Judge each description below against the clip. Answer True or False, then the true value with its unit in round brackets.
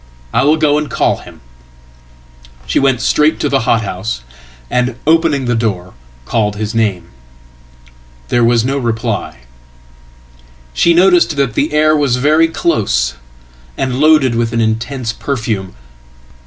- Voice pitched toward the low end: True (115 Hz)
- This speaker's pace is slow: True (125 wpm)